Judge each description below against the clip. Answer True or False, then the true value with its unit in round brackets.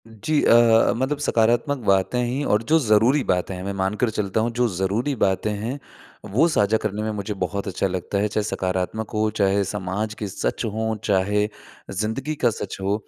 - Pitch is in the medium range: False (105 Hz)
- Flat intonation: False (3.1 semitones)